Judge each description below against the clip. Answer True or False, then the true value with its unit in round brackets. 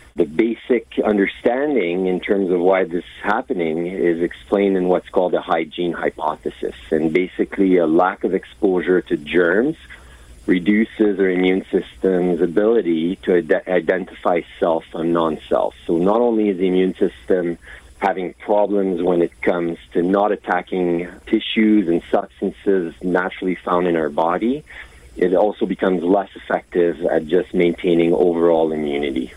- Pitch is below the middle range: True (90 Hz)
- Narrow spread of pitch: True (2.3 semitones)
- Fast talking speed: False (145 wpm)